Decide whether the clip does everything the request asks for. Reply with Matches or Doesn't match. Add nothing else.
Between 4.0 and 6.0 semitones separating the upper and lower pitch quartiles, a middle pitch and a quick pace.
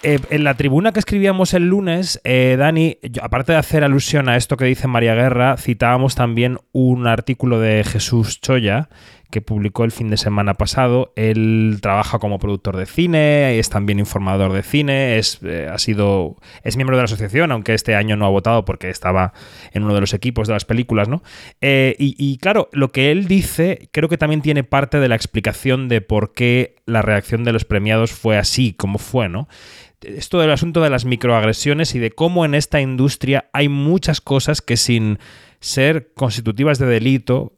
Doesn't match